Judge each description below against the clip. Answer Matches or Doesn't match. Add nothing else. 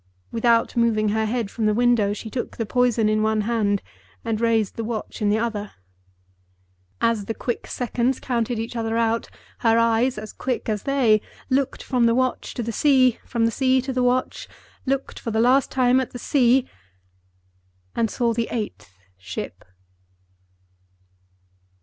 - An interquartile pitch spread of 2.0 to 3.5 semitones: Matches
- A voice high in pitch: Matches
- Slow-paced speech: Doesn't match